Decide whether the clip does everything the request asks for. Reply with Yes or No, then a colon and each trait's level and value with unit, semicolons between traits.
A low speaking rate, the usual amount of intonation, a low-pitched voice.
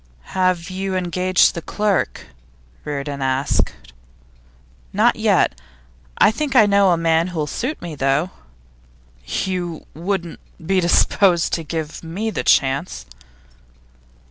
No: slow, 115 wpm; average, 3.6 semitones; medium, 175 Hz